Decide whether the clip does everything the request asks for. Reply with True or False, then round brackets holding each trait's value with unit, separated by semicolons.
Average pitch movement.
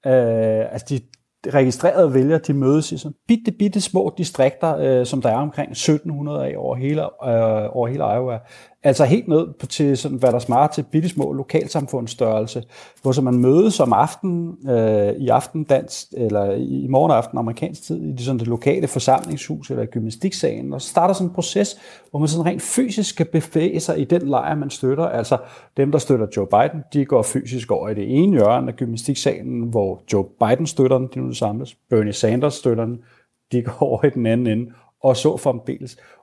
True (4.5 semitones)